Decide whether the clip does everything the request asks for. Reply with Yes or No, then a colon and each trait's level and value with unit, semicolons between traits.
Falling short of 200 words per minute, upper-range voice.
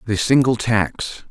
No: average, 140 wpm; low, 110 Hz